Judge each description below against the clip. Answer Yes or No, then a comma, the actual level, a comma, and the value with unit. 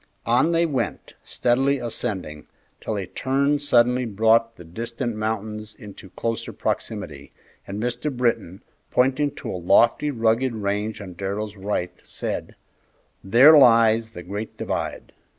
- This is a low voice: Yes, low, 115 Hz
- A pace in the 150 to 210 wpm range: No, slow, 135 wpm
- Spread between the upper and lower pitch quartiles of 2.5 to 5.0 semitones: Yes, average, 3.5 semitones